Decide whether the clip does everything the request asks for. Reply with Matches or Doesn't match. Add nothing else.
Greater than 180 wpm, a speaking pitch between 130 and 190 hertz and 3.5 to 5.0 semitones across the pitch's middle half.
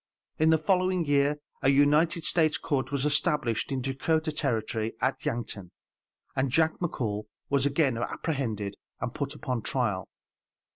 Doesn't match